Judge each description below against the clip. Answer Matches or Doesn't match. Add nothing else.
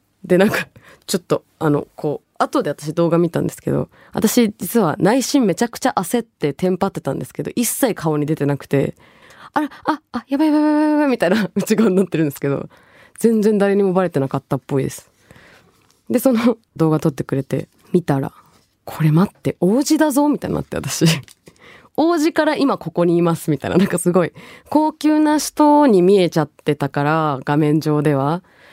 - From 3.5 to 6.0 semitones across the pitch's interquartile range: Doesn't match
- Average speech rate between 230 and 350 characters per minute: Doesn't match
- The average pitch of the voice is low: Doesn't match